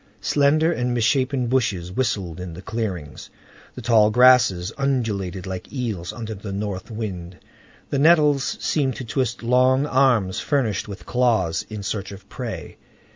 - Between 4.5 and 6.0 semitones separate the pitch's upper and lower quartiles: Yes, average, 5.2 semitones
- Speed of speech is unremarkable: Yes, average, 145 wpm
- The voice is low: Yes, low, 115 Hz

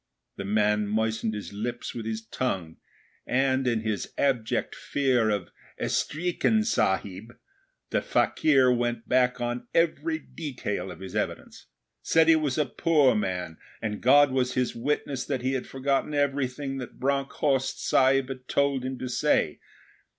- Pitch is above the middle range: No, low, 125 Hz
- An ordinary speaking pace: Yes, average, 150 wpm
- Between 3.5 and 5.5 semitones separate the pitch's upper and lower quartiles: Yes, average, 3.8 semitones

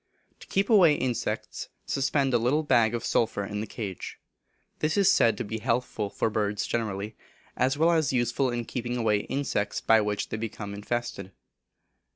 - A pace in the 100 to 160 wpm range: No, average, 175 wpm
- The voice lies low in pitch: Yes, low, 120 Hz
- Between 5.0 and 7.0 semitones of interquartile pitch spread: No, average, 4.1 semitones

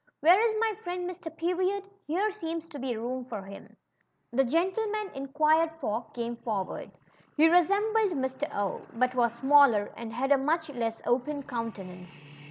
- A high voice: Yes, very high, 285 Hz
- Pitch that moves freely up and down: Yes, wide, 6.9 semitones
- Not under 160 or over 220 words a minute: Yes, average, 170 wpm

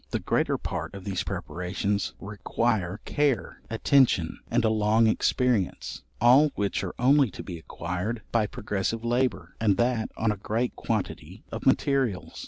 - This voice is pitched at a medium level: No, low, 110 Hz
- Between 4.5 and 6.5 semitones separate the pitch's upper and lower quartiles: No, average, 3.6 semitones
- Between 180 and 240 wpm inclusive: No, average, 150 wpm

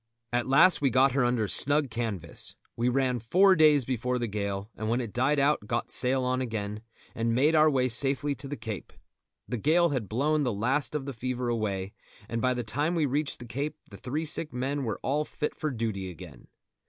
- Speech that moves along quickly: Yes, fast, 215 wpm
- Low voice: Yes, low, 125 Hz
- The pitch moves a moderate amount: Yes, average, 4.1 semitones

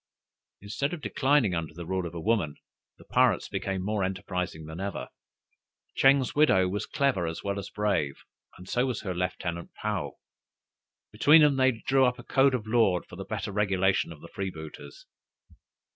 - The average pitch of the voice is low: Yes, low, 100 Hz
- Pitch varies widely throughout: Yes, wide, 5.8 semitones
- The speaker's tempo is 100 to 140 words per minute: No, average, 175 wpm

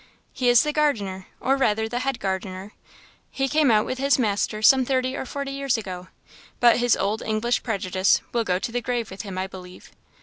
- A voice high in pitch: Yes, high, 230 Hz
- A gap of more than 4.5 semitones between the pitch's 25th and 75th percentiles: Yes, average, 4.9 semitones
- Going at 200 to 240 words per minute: Yes, fast, 205 wpm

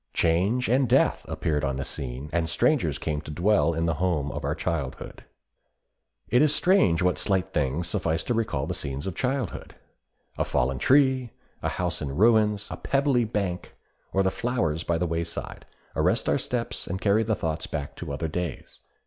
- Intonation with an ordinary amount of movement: No, wide, 6.2 semitones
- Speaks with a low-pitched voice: Yes, very low, 85 Hz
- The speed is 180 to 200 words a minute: Yes, average, 185 wpm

